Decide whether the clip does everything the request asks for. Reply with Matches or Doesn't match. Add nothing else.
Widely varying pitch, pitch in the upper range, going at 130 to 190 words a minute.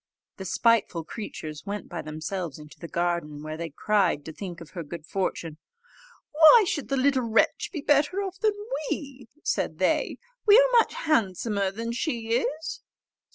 Matches